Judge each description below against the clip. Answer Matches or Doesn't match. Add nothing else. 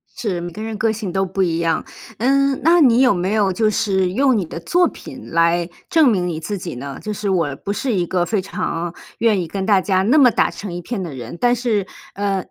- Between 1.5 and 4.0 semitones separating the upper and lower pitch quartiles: Doesn't match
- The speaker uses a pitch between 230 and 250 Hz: Doesn't match